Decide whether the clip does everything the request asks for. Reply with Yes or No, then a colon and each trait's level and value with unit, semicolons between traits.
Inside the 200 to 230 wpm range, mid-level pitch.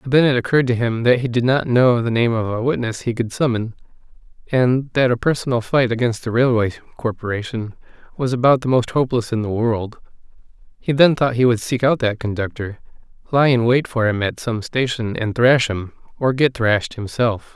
No: fast, 205 wpm; low, 120 Hz